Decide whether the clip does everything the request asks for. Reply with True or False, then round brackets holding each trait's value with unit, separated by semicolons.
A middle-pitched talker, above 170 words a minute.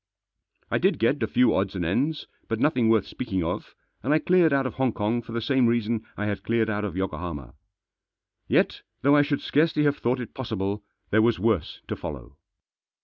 False (115 Hz; 205 wpm)